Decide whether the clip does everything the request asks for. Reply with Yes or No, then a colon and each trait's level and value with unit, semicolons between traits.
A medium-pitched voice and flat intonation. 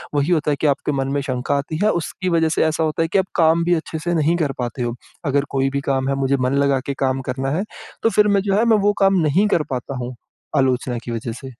No: medium, 145 Hz; average, 4.3 semitones